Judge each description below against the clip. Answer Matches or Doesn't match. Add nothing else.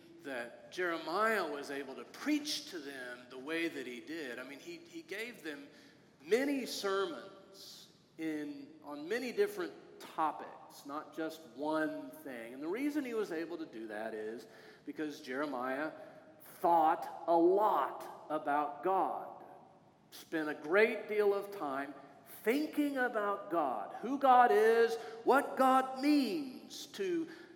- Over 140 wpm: Doesn't match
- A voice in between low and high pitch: Doesn't match